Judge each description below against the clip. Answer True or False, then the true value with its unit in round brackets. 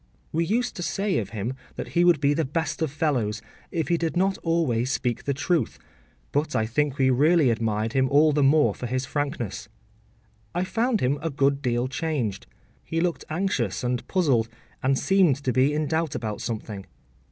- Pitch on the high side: False (140 Hz)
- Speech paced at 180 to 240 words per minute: True (190 wpm)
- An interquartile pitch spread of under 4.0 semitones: False (5.0 semitones)